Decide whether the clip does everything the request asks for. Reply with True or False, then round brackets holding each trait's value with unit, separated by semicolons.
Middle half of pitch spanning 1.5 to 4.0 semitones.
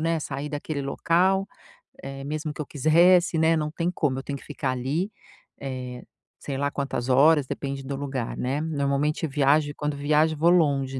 True (2.7 semitones)